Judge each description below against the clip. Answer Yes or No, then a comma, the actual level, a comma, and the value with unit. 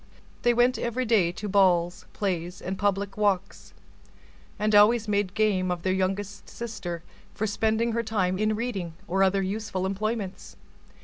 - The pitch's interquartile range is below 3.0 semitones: Yes, narrow, 2.6 semitones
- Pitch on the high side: Yes, high, 200 Hz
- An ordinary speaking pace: Yes, average, 150 wpm